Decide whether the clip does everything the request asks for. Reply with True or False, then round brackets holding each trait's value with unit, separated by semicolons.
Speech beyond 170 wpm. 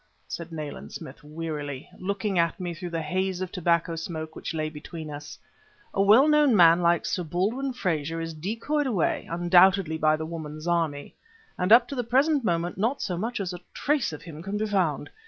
True (195 wpm)